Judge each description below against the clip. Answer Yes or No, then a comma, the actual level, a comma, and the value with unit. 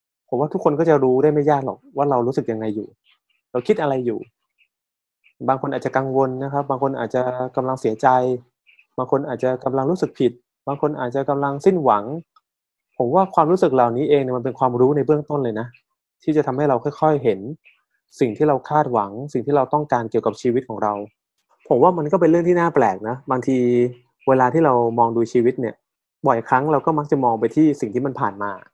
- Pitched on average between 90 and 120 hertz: No, low, 130 Hz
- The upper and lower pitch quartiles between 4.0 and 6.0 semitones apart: No, average, 3.4 semitones